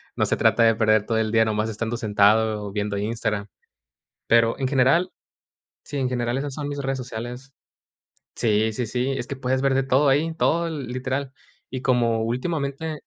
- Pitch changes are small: No, average, 3.4 semitones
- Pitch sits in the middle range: No, low, 125 Hz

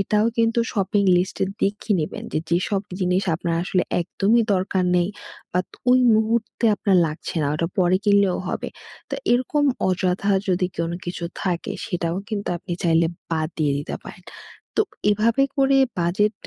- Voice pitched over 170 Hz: Yes, medium, 185 Hz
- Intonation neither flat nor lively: Yes, average, 3.5 semitones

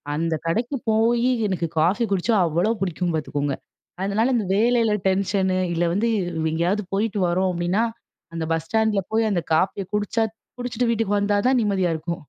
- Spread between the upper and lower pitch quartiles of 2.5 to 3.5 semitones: No, average, 4.3 semitones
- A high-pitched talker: Yes, high, 200 Hz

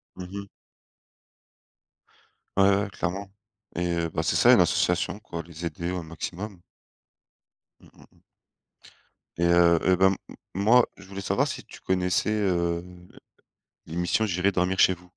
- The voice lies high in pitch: No, very low, 90 Hz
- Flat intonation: Yes, narrow, 2.2 semitones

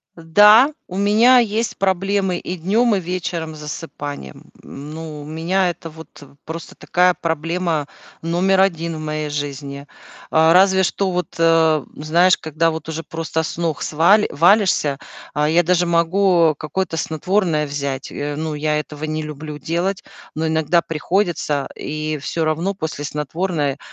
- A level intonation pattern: No, average, 3.1 semitones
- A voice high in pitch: No, medium, 165 Hz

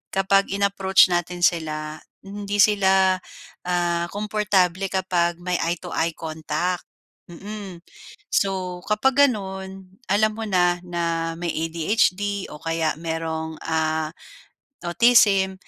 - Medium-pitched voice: Yes, medium, 180 Hz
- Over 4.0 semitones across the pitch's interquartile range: No, average, 3.0 semitones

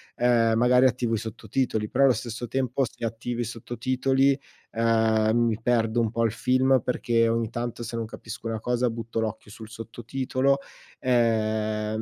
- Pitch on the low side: Yes, low, 115 Hz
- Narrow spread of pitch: Yes, narrow, 1.8 semitones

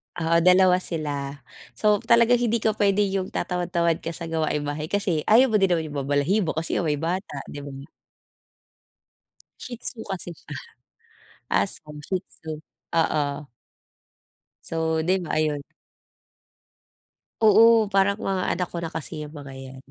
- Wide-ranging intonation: No, average, 4.4 semitones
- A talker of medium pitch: Yes, medium, 170 Hz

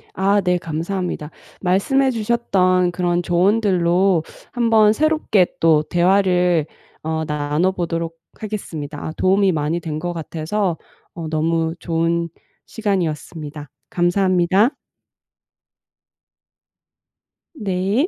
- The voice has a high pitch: No, medium, 180 Hz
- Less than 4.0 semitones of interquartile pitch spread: Yes, average, 3.2 semitones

